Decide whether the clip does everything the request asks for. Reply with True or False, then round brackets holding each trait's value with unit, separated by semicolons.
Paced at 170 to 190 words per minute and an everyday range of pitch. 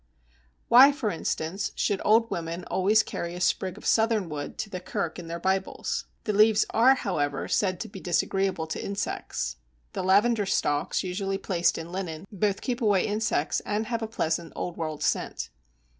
True (175 wpm; 3.9 semitones)